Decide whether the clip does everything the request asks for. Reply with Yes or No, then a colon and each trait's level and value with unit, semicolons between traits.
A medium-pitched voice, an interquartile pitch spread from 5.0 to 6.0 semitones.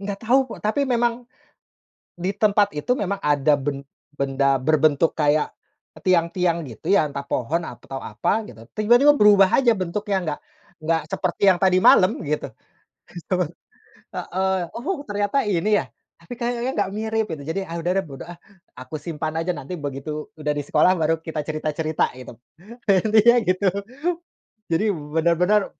Yes: medium, 175 Hz; average, 5.3 semitones